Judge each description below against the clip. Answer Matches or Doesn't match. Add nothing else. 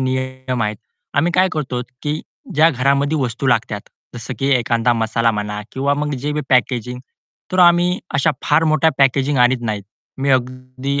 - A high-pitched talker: Doesn't match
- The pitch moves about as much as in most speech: Matches